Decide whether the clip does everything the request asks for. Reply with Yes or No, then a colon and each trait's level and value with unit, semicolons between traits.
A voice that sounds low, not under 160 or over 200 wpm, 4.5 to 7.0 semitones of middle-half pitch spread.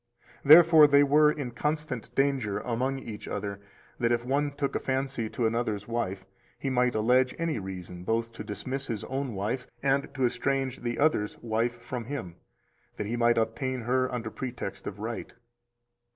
No: low, 125 Hz; average, 170 wpm; average, 3.5 semitones